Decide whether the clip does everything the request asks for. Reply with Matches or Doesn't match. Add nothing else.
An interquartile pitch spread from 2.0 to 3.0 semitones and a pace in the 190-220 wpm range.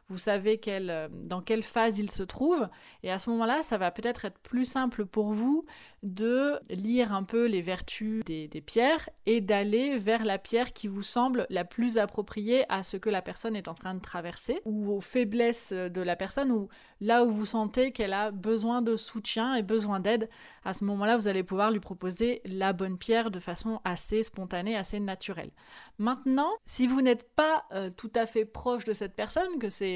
Doesn't match